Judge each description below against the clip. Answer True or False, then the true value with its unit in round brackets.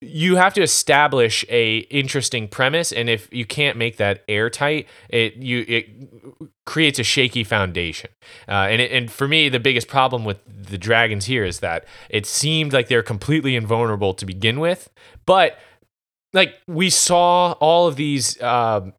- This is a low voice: True (125 Hz)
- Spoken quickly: False (170 wpm)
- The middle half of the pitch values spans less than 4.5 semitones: False (4.9 semitones)